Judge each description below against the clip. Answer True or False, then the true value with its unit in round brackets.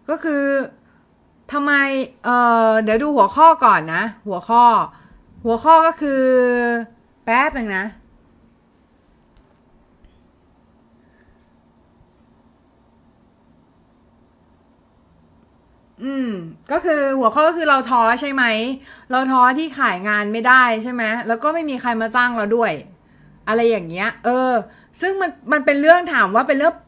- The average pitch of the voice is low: False (250 Hz)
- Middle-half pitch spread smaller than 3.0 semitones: False (4.3 semitones)